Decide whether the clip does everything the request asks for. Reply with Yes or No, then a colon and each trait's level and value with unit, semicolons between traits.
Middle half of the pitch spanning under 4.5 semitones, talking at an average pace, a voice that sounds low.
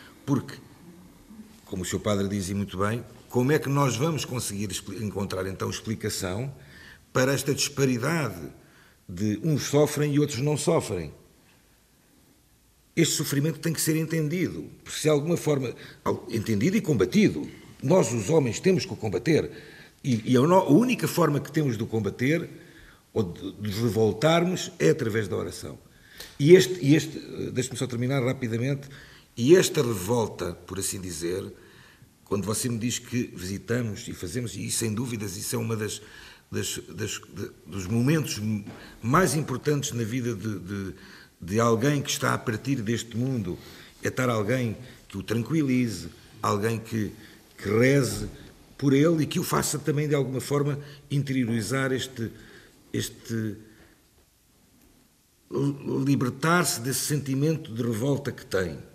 No: average, 5.1 semitones; average, 150 wpm; low, 125 Hz